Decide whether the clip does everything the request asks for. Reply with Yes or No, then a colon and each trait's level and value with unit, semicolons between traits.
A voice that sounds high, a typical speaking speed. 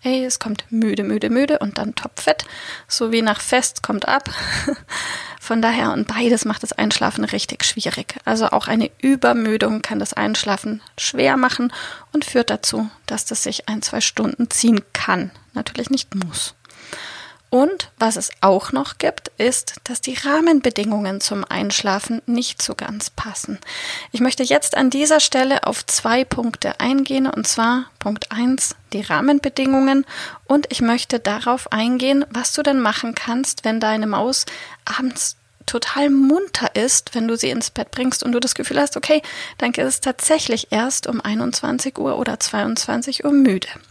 Yes: very high, 250 Hz; average, 165 wpm